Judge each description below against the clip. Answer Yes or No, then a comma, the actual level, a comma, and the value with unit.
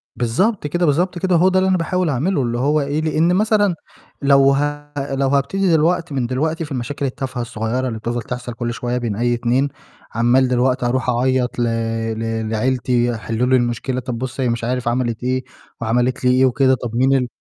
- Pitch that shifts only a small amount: No, average, 3.4 semitones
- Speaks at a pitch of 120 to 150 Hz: Yes, low, 130 Hz